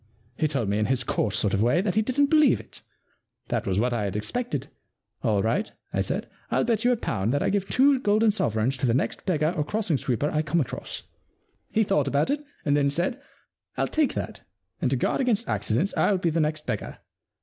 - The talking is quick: Yes, fast, 225 wpm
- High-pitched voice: No, medium, 155 Hz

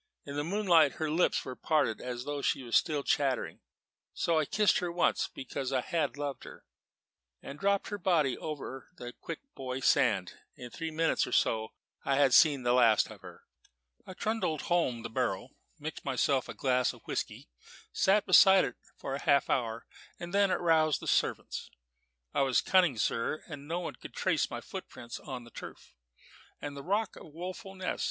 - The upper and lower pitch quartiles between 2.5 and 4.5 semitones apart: No, average, 5.2 semitones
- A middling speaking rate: Yes, average, 185 wpm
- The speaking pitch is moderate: Yes, medium, 145 Hz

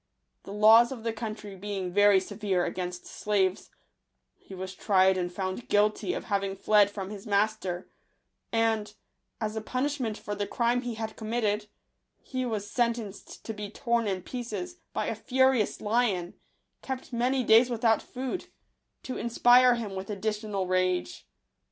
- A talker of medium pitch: No, high, 215 Hz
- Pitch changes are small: No, average, 3.2 semitones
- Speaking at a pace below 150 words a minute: No, average, 155 wpm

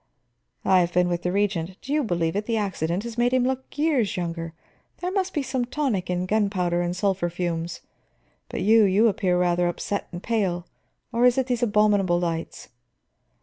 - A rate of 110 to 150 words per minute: No, average, 190 wpm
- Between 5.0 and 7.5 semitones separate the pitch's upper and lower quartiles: Yes, average, 5.3 semitones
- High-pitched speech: Yes, high, 195 Hz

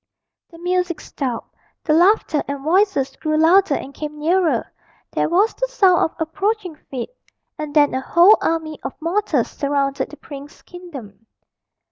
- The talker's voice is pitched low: No, very high, 320 Hz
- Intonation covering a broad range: No, average, 4.3 semitones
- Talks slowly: No, average, 150 wpm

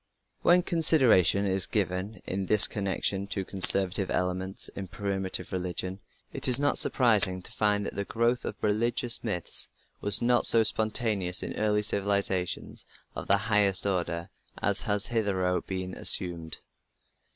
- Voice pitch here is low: Yes, low, 100 Hz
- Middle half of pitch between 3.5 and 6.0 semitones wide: No, narrow, 2.6 semitones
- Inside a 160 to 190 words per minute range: No, average, 145 wpm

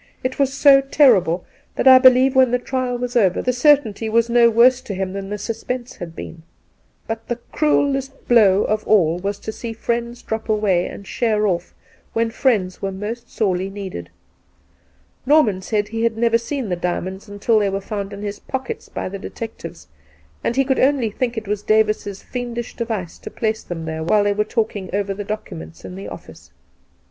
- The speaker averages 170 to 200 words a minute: Yes, average, 195 wpm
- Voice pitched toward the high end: Yes, high, 220 Hz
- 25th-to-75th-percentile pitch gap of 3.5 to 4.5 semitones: Yes, average, 3.8 semitones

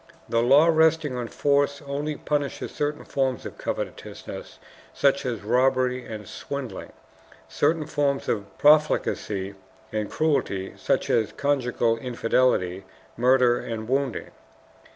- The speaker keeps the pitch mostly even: No, average, 3.9 semitones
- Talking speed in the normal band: No, slow, 115 wpm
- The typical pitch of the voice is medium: No, low, 130 Hz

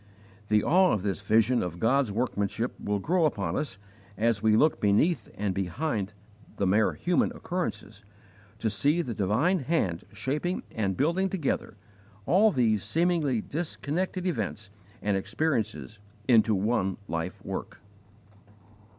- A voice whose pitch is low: Yes, low, 115 Hz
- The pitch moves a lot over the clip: Yes, wide, 7.9 semitones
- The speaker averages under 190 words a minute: Yes, slow, 135 wpm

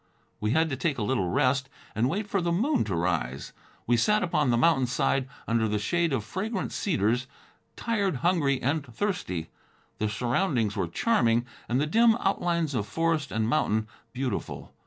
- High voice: No, low, 135 Hz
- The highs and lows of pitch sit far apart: Yes, wide, 7.2 semitones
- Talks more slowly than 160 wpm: No, average, 175 wpm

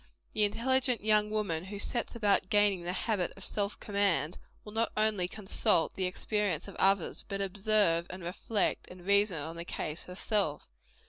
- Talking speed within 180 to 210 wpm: No, average, 170 wpm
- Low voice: No, high, 200 Hz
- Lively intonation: No, average, 2.8 semitones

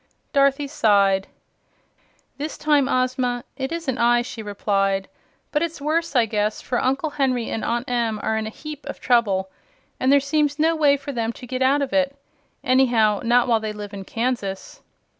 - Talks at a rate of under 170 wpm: No, average, 180 wpm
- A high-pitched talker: Yes, very high, 250 Hz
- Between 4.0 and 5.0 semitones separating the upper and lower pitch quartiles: Yes, average, 4.3 semitones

